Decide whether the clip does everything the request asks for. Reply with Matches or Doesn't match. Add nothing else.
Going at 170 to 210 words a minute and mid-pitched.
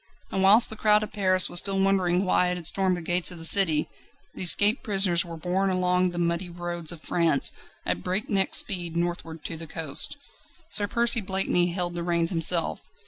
Matches